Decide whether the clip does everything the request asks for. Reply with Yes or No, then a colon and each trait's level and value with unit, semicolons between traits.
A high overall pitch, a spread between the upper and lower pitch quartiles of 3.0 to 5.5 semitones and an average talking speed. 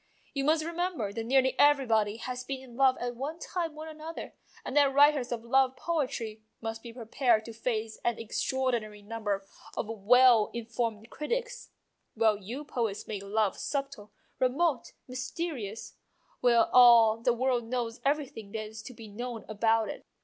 Yes: high, 240 Hz; average, 3.6 semitones; average, 165 wpm